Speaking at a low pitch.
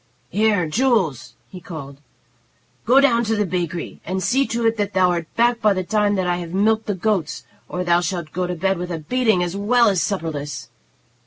No: medium, 185 Hz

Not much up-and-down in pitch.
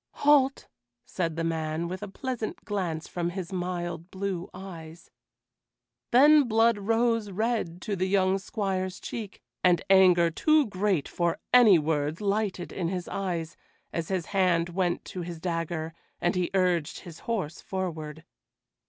No: average, 3.2 semitones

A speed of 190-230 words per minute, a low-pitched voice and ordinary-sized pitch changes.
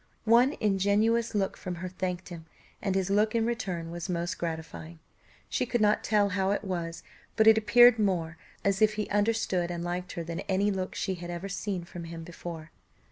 No: average, 195 wpm; high, 190 Hz; average, 3.5 semitones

